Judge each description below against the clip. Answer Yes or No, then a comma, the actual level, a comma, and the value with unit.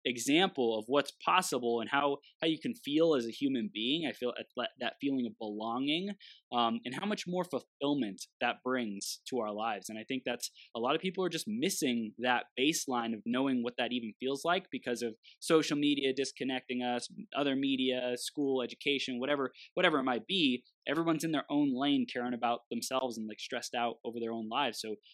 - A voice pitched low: Yes, low, 130 Hz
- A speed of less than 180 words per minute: No, average, 200 wpm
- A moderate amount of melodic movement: Yes, average, 4.9 semitones